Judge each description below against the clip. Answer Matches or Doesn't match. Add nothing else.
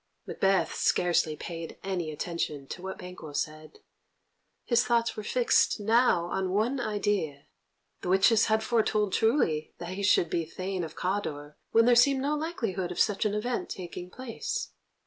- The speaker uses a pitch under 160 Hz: Doesn't match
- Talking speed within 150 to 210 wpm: Matches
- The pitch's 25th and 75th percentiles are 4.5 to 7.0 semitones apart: Matches